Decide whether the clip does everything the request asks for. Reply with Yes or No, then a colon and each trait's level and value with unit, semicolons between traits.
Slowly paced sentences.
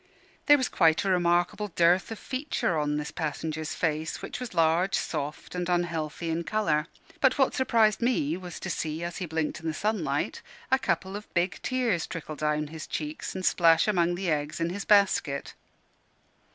No: average, 180 wpm